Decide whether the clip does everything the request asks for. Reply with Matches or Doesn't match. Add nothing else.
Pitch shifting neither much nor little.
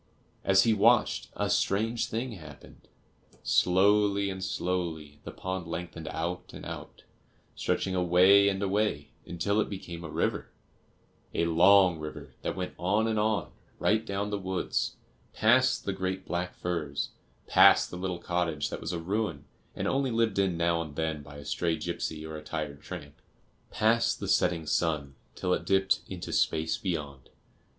Matches